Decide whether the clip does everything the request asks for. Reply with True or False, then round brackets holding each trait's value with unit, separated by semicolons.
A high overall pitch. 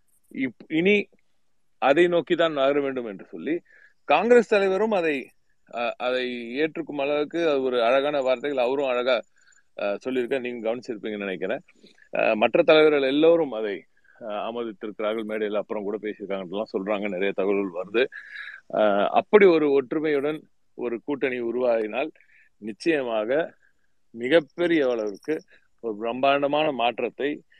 False (135 Hz)